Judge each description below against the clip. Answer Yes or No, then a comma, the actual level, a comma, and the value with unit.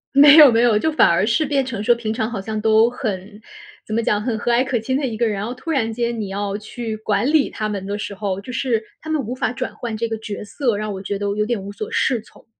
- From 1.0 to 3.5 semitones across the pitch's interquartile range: Yes, average, 3.0 semitones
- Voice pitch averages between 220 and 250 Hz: Yes, high, 225 Hz